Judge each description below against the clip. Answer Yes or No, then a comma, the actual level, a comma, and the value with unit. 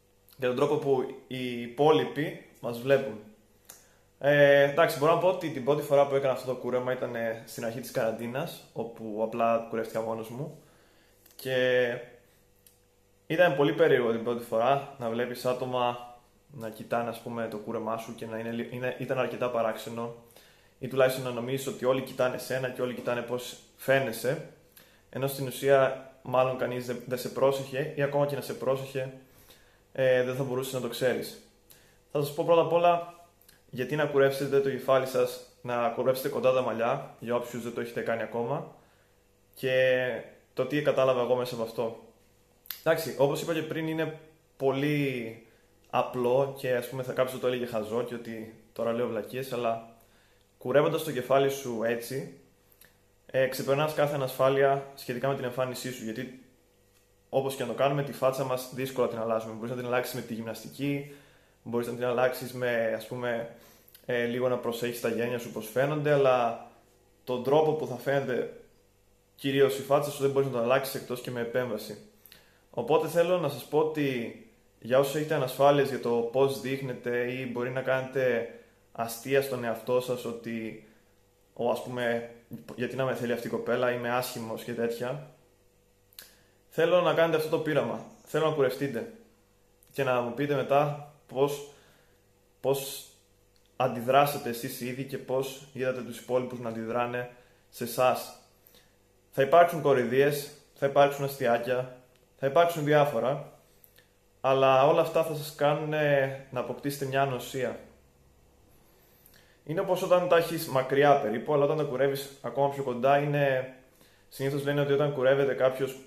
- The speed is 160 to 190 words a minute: Yes, average, 165 wpm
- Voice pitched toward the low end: Yes, low, 125 Hz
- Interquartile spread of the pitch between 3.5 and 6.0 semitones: No, average, 2.8 semitones